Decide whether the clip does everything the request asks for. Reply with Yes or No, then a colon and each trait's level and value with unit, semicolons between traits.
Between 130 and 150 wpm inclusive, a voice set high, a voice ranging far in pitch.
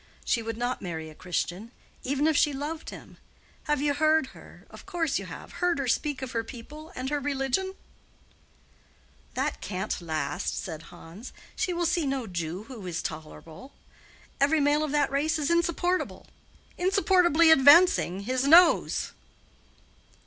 Yes: average, 140 wpm; very high, 275 Hz; wide, 6.6 semitones